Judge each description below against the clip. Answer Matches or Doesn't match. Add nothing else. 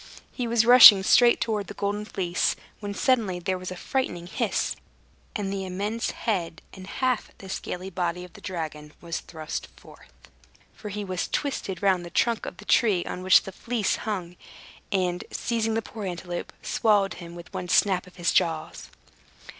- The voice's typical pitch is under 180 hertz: Doesn't match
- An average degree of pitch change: Matches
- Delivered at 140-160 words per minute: Doesn't match